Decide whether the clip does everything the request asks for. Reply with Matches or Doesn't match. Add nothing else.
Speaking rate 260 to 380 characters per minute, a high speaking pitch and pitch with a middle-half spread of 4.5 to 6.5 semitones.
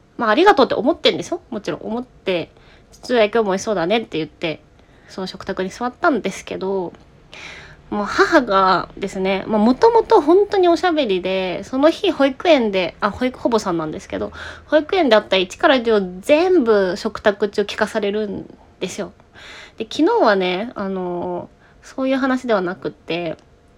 Doesn't match